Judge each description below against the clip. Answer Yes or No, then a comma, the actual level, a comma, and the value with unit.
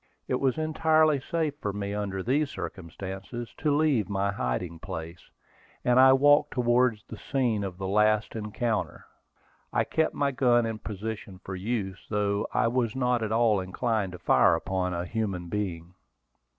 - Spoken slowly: No, average, 165 wpm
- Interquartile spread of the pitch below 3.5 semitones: No, average, 4.8 semitones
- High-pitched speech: No, low, 110 Hz